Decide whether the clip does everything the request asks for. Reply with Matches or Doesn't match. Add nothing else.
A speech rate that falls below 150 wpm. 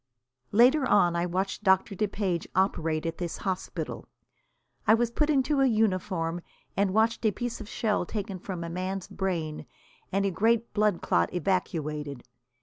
Doesn't match